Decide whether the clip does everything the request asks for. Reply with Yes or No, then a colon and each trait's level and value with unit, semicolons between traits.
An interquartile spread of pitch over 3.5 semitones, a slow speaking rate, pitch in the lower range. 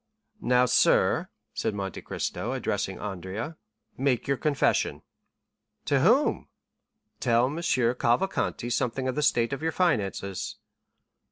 Yes: average, 3.9 semitones; slow, 115 wpm; low, 125 Hz